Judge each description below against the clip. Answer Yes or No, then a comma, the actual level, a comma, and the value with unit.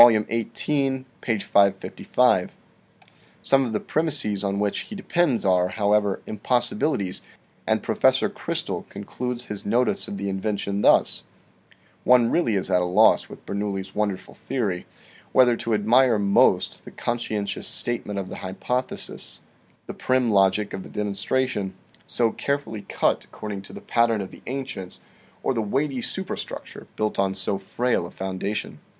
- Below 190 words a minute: Yes, average, 150 wpm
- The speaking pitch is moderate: No, low, 105 Hz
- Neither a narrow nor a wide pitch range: Yes, average, 4.0 semitones